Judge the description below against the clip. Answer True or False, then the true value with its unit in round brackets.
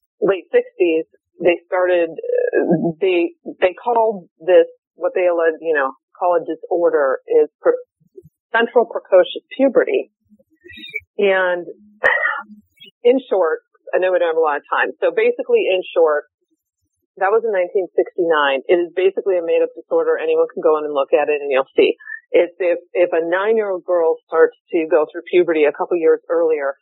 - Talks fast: False (170 wpm)